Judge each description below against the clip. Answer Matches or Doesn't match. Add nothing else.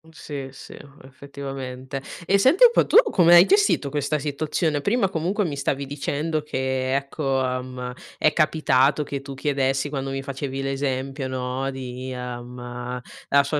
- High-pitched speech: Doesn't match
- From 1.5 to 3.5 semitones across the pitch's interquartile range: Matches